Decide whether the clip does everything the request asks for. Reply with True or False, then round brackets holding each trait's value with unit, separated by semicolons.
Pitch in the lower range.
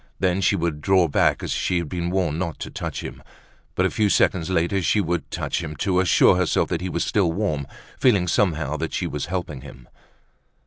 True (85 Hz)